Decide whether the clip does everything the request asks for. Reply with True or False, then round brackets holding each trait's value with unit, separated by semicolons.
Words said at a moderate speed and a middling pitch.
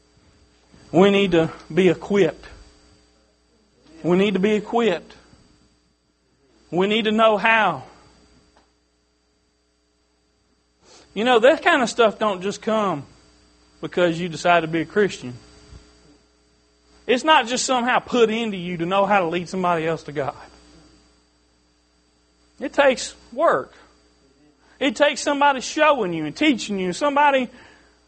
False (125 wpm; 160 Hz)